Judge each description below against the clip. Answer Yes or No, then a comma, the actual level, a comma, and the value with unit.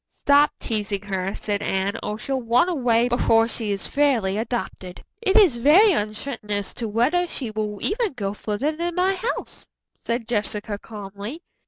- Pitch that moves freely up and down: Yes, wide, 5.9 semitones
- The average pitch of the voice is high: Yes, high, 230 Hz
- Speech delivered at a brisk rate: No, average, 165 wpm